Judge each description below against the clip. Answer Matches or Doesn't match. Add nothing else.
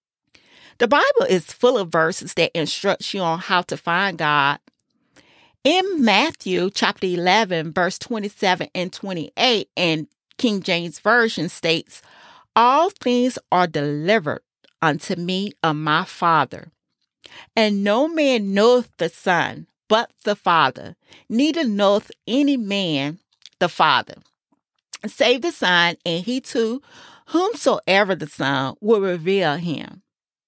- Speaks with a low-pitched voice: Doesn't match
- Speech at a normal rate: Doesn't match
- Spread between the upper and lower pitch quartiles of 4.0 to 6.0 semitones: Matches